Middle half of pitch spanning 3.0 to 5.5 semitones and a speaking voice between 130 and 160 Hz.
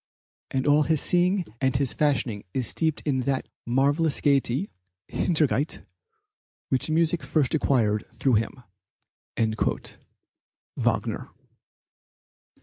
Yes: average, 3.5 semitones; medium, 140 Hz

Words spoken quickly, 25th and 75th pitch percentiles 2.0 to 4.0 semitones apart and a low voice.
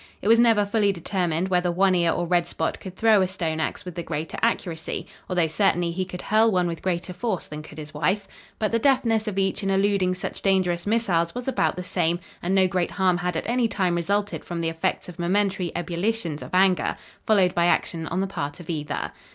No: fast, 225 wpm; average, 2.8 semitones; medium, 185 Hz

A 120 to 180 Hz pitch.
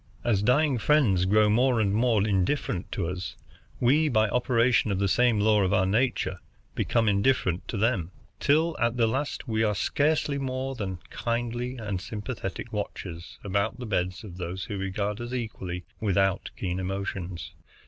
No: low, 110 Hz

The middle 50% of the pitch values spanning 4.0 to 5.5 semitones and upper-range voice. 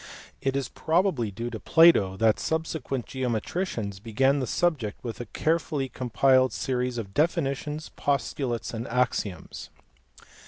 No: average, 4.5 semitones; low, 130 Hz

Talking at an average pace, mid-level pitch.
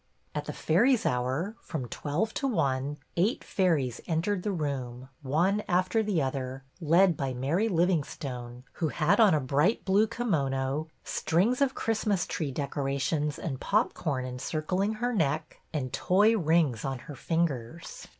Yes: average, 150 wpm; medium, 160 Hz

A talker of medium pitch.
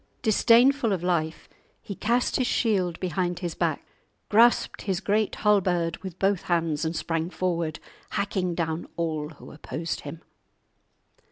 Yes: medium, 180 Hz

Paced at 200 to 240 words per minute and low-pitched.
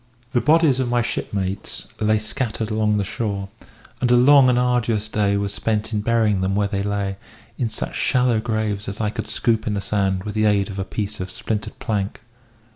Yes: fast, 205 wpm; low, 105 Hz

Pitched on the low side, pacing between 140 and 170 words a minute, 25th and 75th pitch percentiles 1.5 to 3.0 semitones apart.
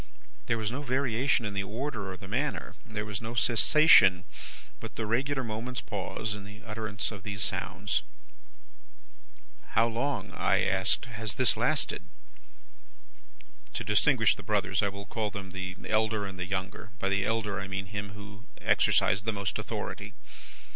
Yes: low, 105 Hz; average, 160 wpm; average, 2.7 semitones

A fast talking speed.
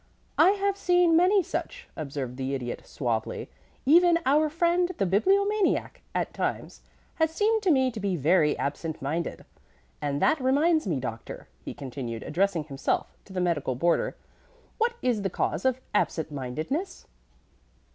No: average, 150 wpm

